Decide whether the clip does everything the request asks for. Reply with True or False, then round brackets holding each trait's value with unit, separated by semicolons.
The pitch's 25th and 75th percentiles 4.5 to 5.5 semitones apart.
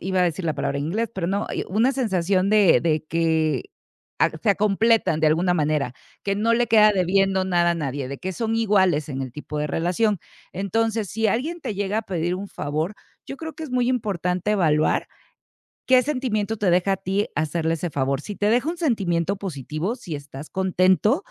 True (5.0 semitones)